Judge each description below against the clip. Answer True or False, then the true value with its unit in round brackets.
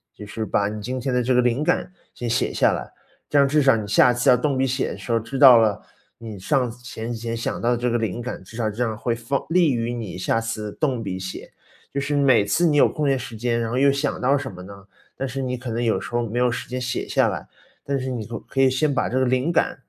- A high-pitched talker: False (120 Hz)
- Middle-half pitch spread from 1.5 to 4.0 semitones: True (2.9 semitones)